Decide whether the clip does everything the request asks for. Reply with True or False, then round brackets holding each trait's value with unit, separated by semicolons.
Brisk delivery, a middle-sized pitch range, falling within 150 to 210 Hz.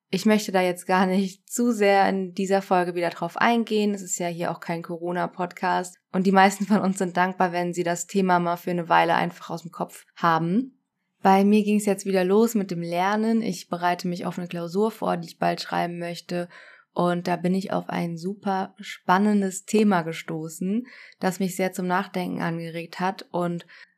False (205 wpm; 2.1 semitones; 185 Hz)